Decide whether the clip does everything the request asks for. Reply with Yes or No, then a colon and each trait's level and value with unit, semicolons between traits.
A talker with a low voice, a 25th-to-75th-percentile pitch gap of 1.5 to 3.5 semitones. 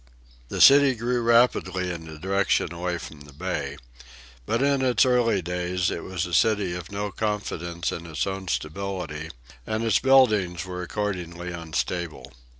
No: very low, 90 Hz; average, 4.1 semitones